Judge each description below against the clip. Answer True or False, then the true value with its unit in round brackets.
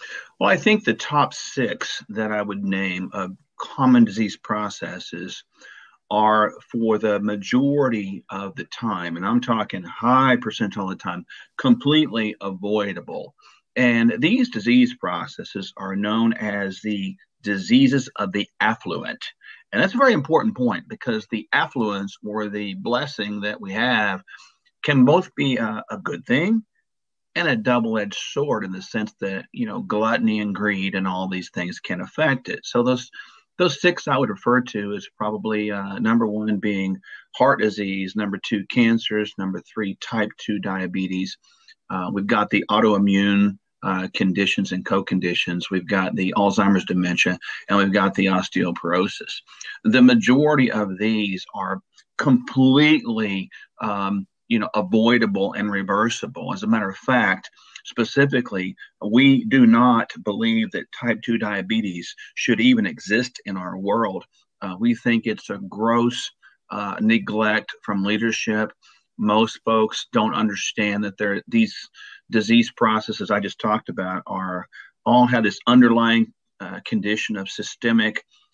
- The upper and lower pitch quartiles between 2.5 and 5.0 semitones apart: True (4.5 semitones)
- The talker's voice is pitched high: False (110 Hz)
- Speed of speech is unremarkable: True (145 wpm)